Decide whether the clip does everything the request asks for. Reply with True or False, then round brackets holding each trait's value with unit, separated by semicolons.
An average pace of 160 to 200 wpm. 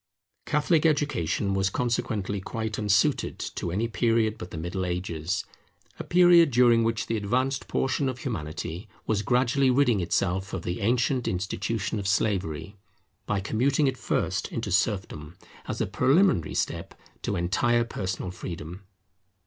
False (140 wpm)